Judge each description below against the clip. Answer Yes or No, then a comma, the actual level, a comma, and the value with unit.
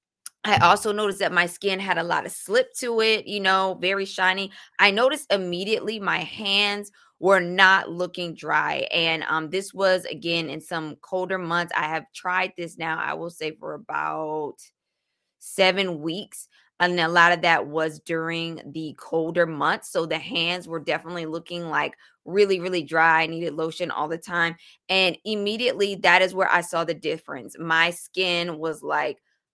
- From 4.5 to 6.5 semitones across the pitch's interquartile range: No, average, 2.7 semitones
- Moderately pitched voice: Yes, medium, 175 Hz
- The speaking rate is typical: Yes, average, 175 wpm